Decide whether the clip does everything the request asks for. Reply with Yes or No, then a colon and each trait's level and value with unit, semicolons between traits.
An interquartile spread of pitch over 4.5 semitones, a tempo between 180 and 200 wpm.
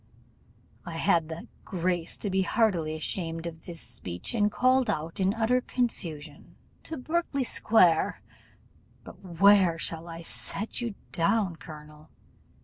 No: average, 5.1 semitones; slow, 135 wpm